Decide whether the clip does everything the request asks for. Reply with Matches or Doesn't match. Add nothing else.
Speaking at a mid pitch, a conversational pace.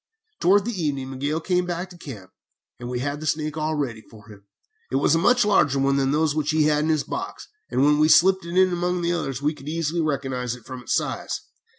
Doesn't match